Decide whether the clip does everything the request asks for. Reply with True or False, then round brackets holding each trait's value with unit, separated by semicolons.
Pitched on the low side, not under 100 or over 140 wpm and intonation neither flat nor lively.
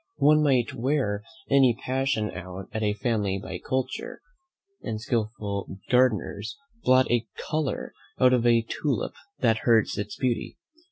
True (115 Hz; 135 wpm; 3.7 semitones)